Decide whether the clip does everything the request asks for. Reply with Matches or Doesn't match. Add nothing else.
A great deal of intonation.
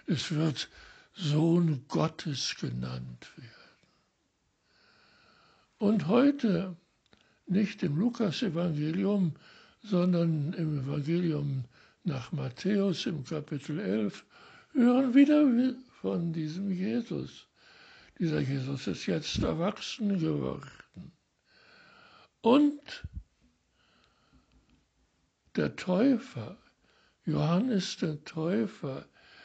Matches